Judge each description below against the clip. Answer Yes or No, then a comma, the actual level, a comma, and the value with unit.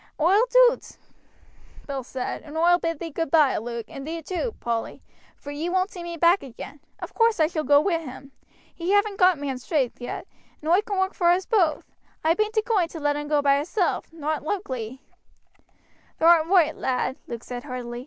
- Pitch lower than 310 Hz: No, very high, 320 Hz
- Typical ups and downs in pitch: Yes, average, 4.7 semitones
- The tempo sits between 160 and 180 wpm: No, average, 200 wpm